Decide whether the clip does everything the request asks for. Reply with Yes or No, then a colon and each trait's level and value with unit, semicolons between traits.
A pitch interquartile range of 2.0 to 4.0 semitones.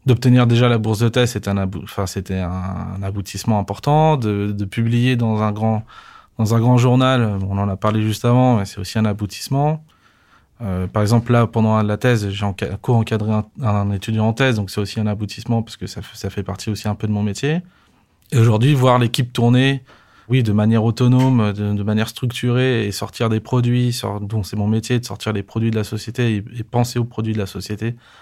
Yes: average, 2.9 semitones